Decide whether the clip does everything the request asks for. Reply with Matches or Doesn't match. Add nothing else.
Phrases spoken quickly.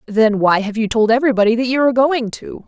Matches